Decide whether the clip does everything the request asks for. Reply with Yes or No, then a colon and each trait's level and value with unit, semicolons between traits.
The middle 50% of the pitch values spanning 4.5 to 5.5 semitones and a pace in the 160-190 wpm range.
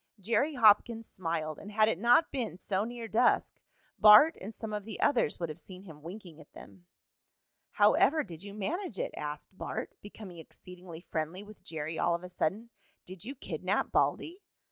Yes: average, 5.0 semitones; average, 185 wpm